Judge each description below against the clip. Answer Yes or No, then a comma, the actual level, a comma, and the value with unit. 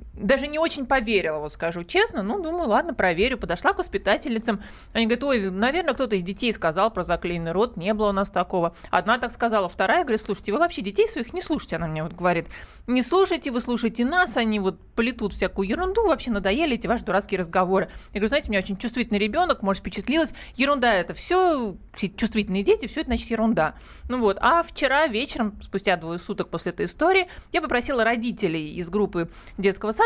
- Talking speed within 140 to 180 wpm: No, fast, 200 wpm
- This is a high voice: Yes, high, 225 Hz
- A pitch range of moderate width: No, wide, 5.7 semitones